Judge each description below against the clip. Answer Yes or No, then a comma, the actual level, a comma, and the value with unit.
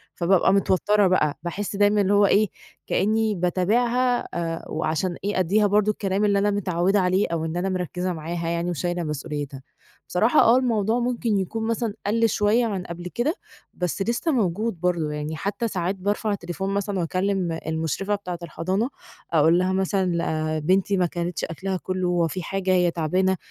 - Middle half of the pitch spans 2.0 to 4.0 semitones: Yes, average, 3.2 semitones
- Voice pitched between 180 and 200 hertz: Yes, medium, 185 Hz